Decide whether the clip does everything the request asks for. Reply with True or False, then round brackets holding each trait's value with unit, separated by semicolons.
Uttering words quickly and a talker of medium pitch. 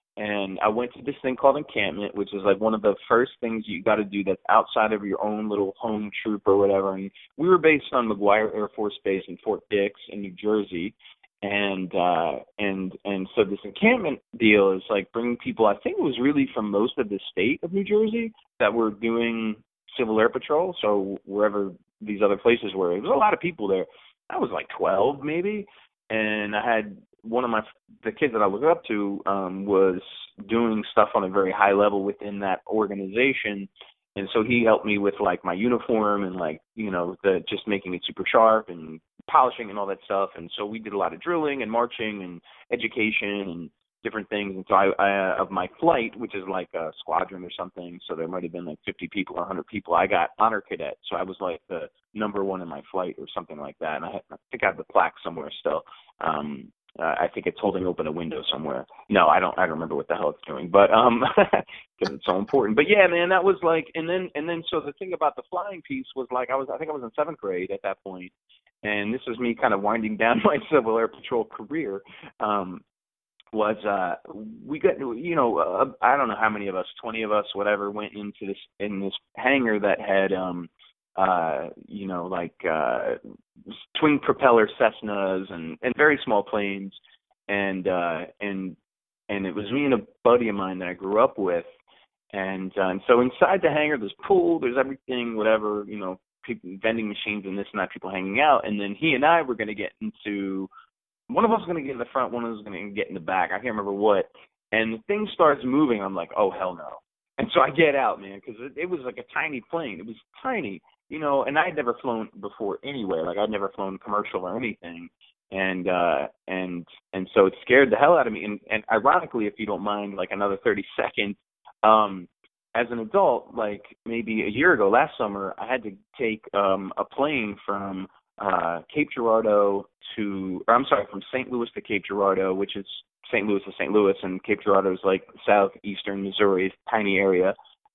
False (220 wpm; 105 Hz)